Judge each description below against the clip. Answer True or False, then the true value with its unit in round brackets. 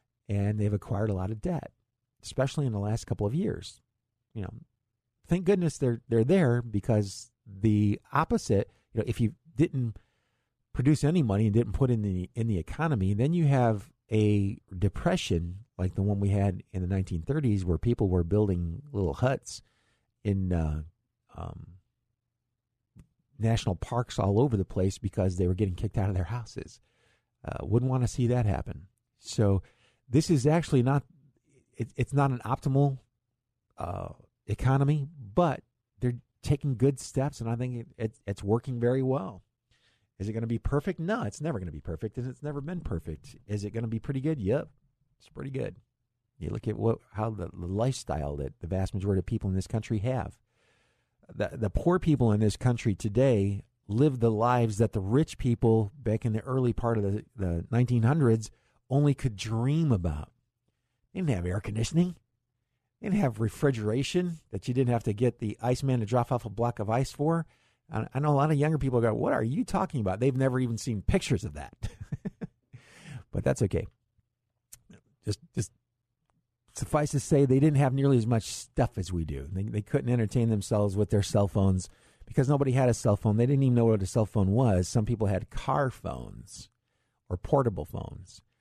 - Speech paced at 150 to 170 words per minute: False (190 wpm)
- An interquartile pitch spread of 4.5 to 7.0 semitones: False (4.1 semitones)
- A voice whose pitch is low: True (115 Hz)